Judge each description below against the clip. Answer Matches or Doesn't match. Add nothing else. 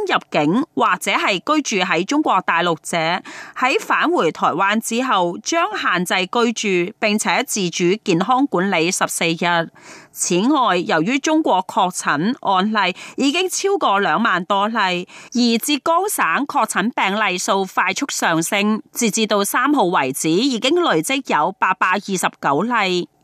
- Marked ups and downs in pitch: Matches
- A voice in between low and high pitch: Doesn't match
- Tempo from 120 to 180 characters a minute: Doesn't match